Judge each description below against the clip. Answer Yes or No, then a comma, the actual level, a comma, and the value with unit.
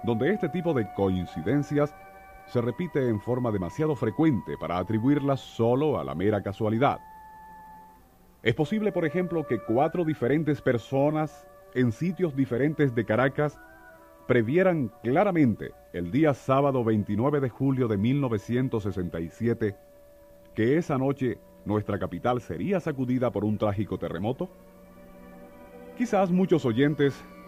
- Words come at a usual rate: No, slow, 120 wpm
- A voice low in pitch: Yes, low, 130 Hz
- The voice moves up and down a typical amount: No, wide, 6.6 semitones